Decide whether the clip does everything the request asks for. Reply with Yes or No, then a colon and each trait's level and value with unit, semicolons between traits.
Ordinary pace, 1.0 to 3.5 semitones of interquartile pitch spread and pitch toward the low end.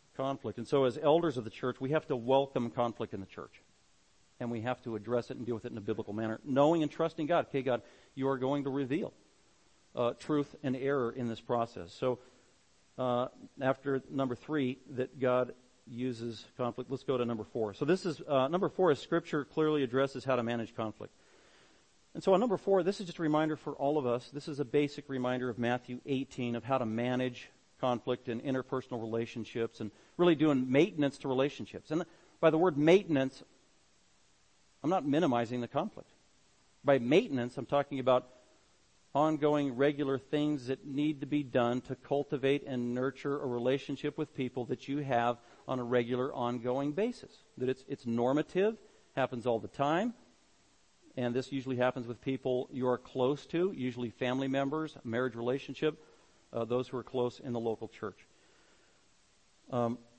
Yes: average, 180 wpm; average, 2.9 semitones; low, 130 Hz